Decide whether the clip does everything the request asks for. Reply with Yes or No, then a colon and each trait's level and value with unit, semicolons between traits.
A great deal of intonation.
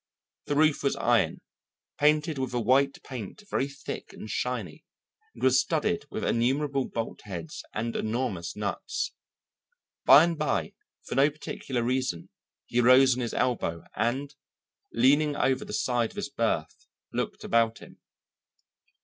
No: average, 3.4 semitones